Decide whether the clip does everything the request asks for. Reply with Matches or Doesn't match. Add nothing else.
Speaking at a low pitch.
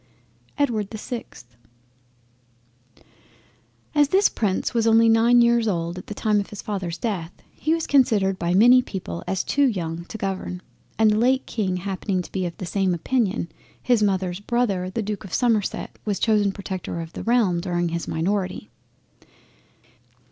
Doesn't match